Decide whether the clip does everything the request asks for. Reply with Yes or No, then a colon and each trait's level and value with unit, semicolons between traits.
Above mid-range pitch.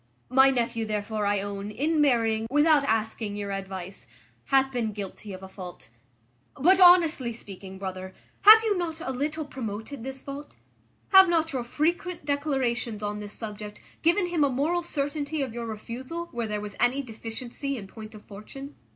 Yes: high, 245 Hz